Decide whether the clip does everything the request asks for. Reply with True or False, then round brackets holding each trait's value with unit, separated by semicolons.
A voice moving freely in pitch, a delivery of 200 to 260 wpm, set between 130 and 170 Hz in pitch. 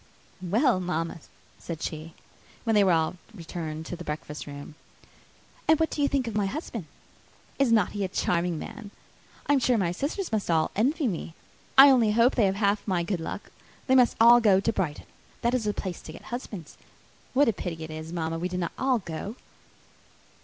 False (6.0 semitones; 205 wpm; 195 Hz)